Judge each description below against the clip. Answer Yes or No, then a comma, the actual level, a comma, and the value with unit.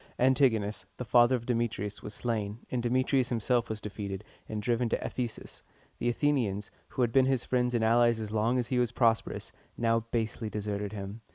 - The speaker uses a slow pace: No, average, 185 wpm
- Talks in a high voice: No, low, 115 Hz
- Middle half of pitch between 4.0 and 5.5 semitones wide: No, narrow, 2.6 semitones